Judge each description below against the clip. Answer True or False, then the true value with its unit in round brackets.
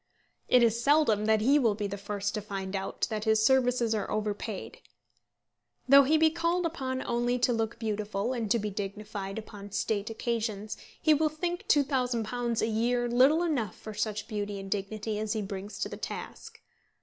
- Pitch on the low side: False (220 Hz)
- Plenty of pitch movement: False (3.3 semitones)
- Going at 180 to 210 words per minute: True (185 wpm)